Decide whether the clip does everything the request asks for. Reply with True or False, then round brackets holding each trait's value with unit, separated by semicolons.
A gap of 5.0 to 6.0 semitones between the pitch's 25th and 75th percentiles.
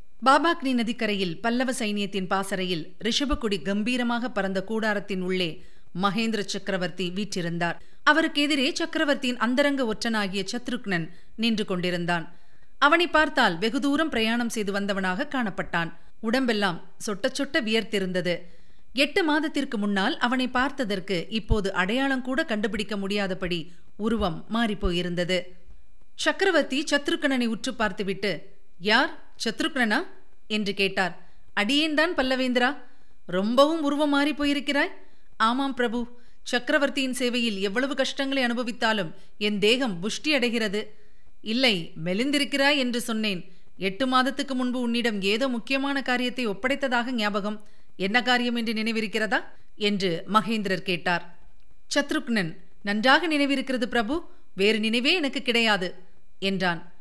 True (5.3 semitones)